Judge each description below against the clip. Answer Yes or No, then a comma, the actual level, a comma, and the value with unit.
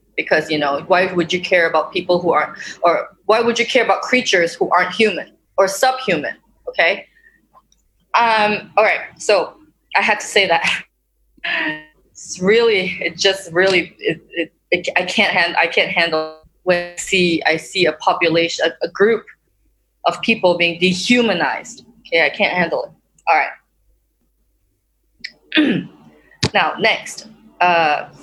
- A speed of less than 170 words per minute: Yes, average, 155 wpm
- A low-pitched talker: No, medium, 180 Hz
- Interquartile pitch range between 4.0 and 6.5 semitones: Yes, average, 4.7 semitones